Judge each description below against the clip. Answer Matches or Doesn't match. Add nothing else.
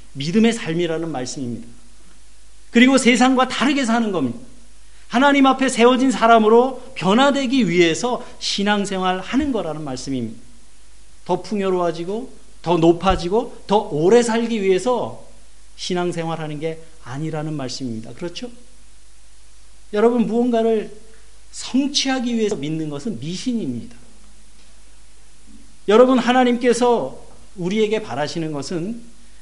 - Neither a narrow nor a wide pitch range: Doesn't match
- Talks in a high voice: Matches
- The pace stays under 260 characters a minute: Doesn't match